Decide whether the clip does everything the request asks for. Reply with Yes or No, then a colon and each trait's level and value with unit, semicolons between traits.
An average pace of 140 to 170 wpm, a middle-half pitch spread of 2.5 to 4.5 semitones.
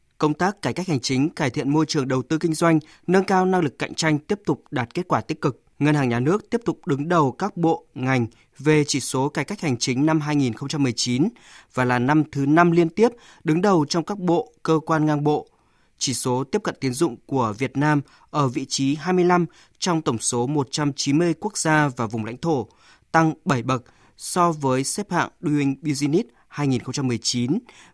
No: average, 205 wpm; average, 4.0 semitones